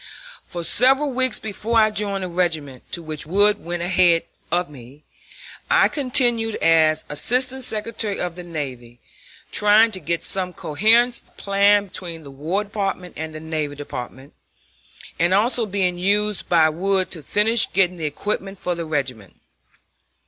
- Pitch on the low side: No, medium, 180 Hz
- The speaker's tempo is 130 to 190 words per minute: Yes, average, 155 wpm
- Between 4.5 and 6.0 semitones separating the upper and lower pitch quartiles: Yes, average, 4.8 semitones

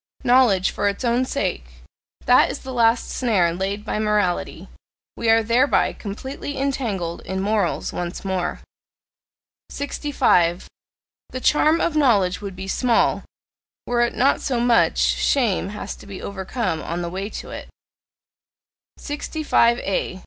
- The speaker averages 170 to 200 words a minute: No, slow, 135 wpm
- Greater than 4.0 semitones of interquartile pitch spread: Yes, average, 5.0 semitones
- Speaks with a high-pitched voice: Yes, high, 215 Hz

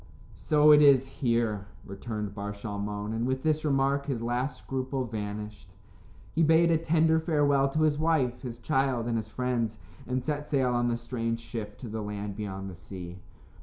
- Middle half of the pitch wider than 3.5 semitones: Yes, average, 5.0 semitones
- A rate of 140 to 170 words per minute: No, average, 180 wpm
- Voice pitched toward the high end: No, low, 120 Hz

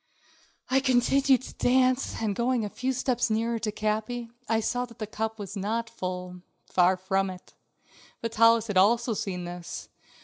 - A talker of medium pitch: No, high, 225 Hz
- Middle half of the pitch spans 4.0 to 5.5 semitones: No, average, 3.6 semitones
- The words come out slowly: No, average, 160 wpm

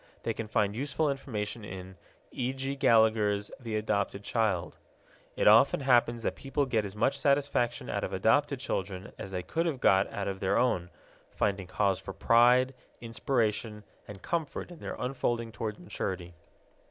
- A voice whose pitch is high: No, low, 110 Hz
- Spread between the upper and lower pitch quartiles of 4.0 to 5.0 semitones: Yes, average, 4.4 semitones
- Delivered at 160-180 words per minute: Yes, average, 165 wpm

